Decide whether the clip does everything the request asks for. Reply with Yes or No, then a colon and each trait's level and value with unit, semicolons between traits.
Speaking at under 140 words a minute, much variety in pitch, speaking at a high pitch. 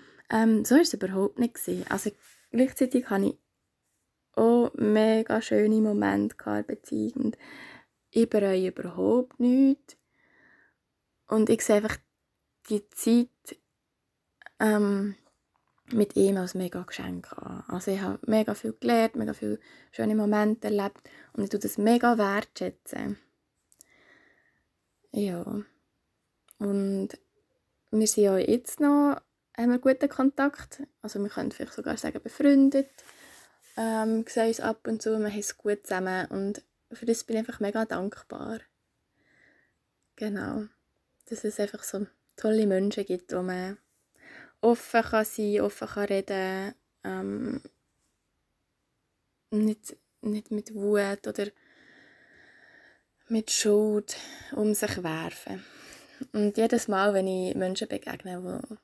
No: slow, 125 wpm; average, 2.9 semitones; high, 215 Hz